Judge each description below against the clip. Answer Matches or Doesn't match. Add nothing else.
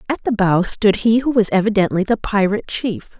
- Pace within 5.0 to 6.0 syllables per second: Matches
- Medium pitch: Doesn't match